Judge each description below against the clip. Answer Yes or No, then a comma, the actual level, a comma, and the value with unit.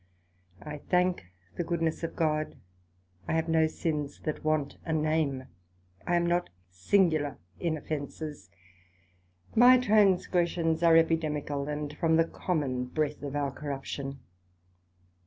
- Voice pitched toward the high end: No, medium, 155 Hz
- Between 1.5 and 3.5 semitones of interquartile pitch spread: Yes, narrow, 2.6 semitones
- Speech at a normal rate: No, slow, 125 wpm